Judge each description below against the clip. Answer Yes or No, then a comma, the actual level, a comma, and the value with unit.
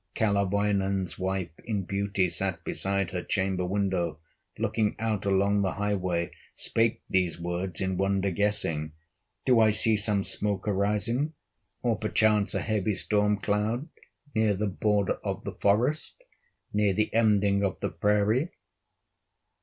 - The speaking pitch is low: Yes, low, 100 Hz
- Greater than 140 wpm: No, slow, 135 wpm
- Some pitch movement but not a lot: No, narrow, 1.9 semitones